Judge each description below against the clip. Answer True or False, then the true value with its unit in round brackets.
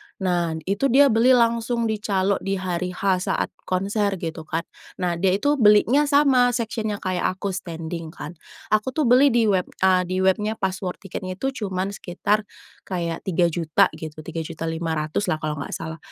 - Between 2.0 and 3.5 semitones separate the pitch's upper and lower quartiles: False (4.3 semitones)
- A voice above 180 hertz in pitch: True (190 Hz)